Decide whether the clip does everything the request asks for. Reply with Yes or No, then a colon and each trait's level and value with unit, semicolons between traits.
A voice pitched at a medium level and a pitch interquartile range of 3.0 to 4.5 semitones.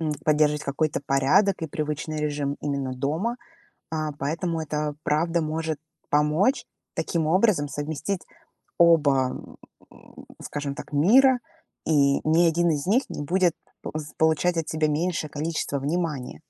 No: medium, 155 Hz; narrow, 2.5 semitones